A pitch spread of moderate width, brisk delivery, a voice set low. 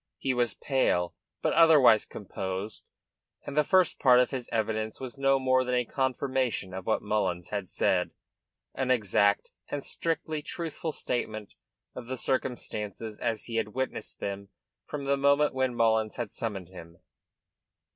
No: average, 4.0 semitones; average, 155 wpm; low, 120 Hz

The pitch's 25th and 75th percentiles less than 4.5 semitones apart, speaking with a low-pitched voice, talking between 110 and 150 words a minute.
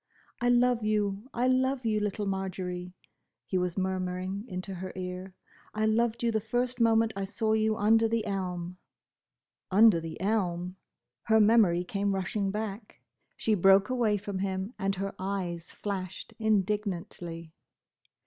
No: average, 3.0 semitones; high, 200 Hz; average, 145 wpm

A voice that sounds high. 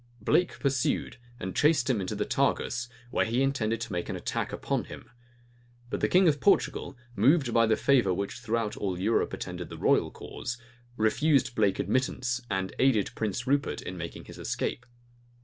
No: low, 120 Hz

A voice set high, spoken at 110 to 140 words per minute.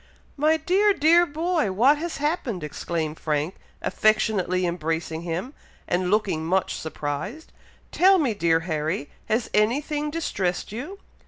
Yes: high, 210 Hz; slow, 135 wpm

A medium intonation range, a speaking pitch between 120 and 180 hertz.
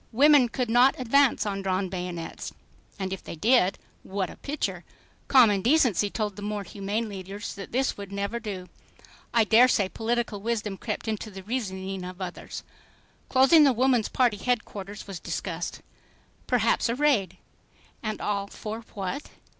No: average, 3.8 semitones; high, 210 Hz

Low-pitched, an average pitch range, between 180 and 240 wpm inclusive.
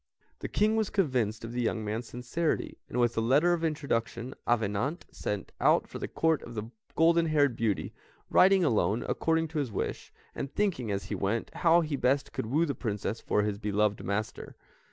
No: low, 125 Hz; wide, 6.8 semitones; average, 190 wpm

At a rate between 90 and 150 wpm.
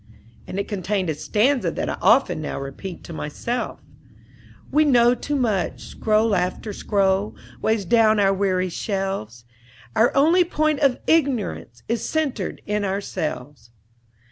Yes: average, 140 wpm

